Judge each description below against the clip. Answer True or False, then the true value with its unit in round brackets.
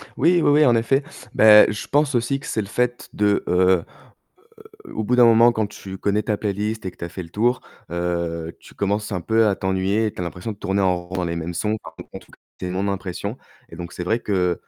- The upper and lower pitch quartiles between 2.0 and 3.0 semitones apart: False (3.9 semitones)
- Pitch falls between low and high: False (100 Hz)